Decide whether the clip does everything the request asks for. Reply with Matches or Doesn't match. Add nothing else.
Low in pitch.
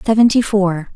Doesn't match